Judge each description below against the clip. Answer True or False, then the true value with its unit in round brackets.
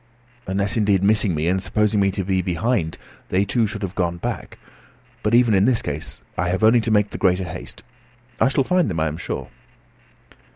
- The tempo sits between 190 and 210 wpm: True (205 wpm)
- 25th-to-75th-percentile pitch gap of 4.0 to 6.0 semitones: False (3.2 semitones)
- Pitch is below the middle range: True (100 Hz)